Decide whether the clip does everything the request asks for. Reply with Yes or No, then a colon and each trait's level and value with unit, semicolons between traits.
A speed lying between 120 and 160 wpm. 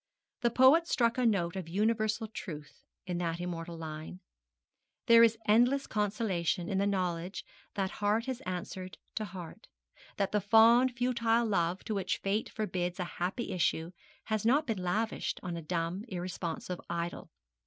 Yes: average, 155 wpm